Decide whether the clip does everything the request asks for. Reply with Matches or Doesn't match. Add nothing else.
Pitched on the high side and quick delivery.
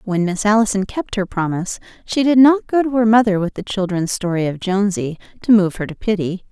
Matches